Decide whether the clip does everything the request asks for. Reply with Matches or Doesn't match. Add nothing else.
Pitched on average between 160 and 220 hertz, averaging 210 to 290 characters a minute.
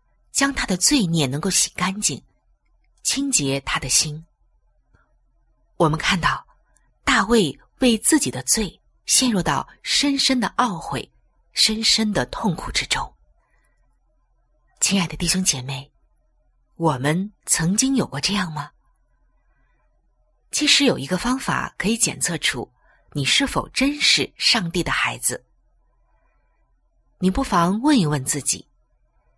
Doesn't match